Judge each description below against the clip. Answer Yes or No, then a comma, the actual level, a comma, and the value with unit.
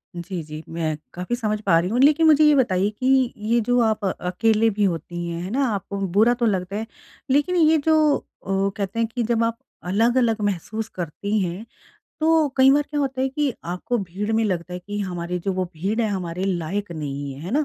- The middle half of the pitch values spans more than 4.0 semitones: Yes, average, 5.1 semitones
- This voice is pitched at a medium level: No, high, 210 Hz